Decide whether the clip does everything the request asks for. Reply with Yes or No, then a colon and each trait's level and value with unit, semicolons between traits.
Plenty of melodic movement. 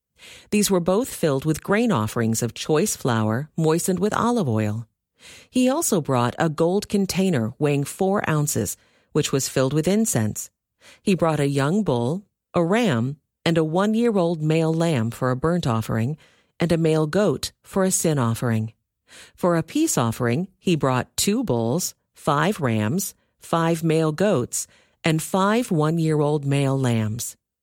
Yes: wide, 7.2 semitones